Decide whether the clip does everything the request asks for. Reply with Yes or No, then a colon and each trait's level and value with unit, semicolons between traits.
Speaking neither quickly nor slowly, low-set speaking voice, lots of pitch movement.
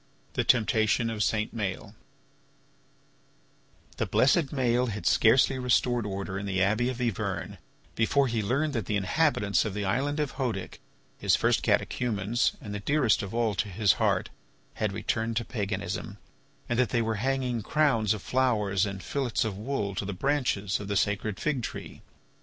No: average, 170 wpm; low, 110 Hz; average, 3.8 semitones